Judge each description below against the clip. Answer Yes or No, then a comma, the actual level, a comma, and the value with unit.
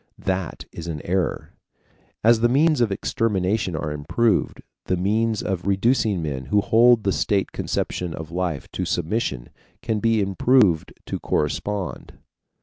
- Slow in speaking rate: No, average, 145 wpm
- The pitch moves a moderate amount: Yes, average, 4.8 semitones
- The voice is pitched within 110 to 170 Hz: No, very low, 95 Hz